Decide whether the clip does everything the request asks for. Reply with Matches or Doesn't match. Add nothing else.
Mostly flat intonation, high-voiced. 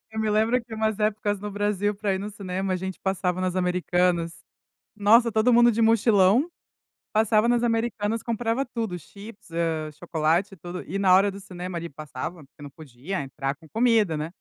Doesn't match